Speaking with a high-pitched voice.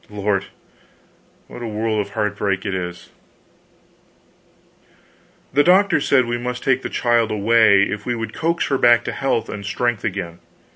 No: low, 115 Hz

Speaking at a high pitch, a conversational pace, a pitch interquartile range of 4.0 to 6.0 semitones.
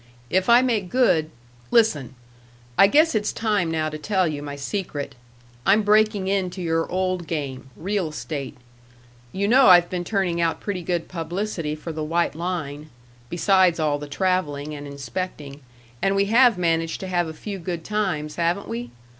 No: medium, 175 Hz; average, 170 wpm; average, 4.3 semitones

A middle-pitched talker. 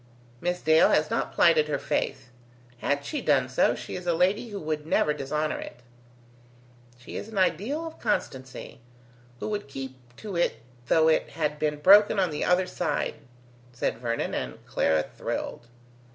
Yes: medium, 155 Hz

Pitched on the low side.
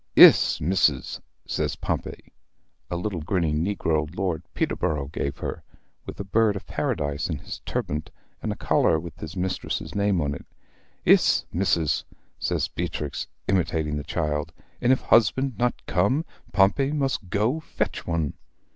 Yes: very low, 85 Hz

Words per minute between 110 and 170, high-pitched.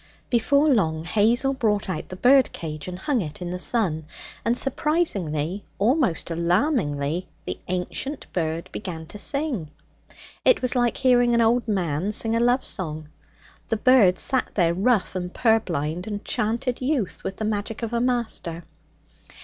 Yes: average, 155 wpm; high, 210 Hz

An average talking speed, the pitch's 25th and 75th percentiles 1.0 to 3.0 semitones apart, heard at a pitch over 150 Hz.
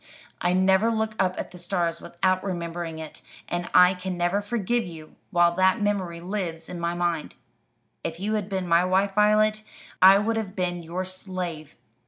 Yes: average, 180 wpm; narrow, 2.5 semitones; medium, 185 Hz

